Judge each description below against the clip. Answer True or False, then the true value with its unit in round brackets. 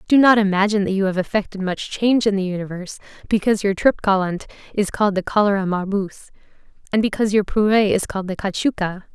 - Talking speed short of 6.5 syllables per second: False (6.6 syllables/s)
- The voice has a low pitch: False (200 Hz)